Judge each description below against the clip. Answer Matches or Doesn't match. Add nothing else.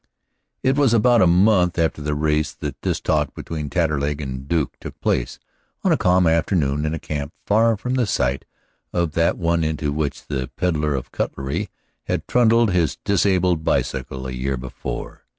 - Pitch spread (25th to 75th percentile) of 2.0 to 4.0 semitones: Doesn't match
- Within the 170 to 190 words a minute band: Matches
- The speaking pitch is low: Matches